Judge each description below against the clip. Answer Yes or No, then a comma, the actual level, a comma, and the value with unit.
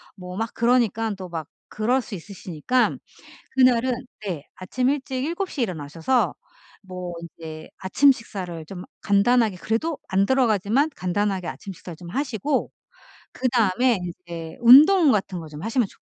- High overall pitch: Yes, high, 210 Hz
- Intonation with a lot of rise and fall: Yes, wide, 5.9 semitones